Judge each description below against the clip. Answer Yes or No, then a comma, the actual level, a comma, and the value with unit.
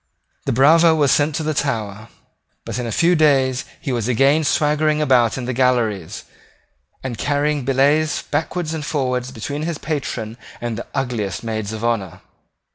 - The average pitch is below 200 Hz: Yes, low, 135 Hz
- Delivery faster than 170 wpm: No, average, 160 wpm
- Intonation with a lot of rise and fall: No, average, 4.3 semitones